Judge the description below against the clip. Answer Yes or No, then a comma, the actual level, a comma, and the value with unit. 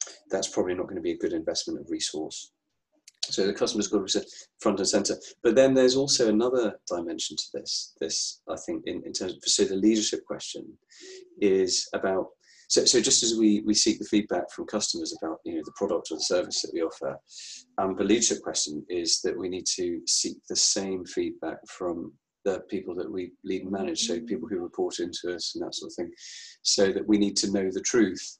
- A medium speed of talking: No, fast, 220 wpm